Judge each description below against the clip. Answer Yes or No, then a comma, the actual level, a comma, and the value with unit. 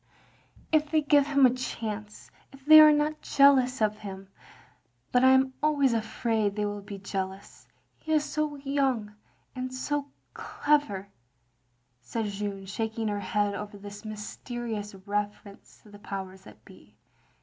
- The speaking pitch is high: Yes, high, 220 Hz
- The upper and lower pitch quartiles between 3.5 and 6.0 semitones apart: Yes, average, 5.2 semitones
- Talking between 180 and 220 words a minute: No, average, 160 wpm